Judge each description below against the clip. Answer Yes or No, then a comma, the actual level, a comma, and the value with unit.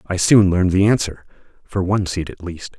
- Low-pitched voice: Yes, very low, 90 Hz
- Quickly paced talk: No, average, 195 wpm